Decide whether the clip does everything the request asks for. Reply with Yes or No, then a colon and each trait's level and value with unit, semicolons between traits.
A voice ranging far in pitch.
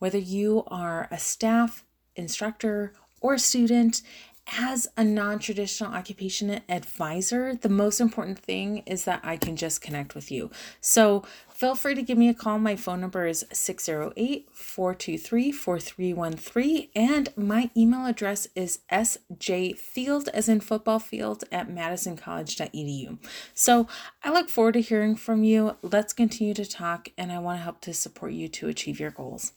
No: average, 4.4 semitones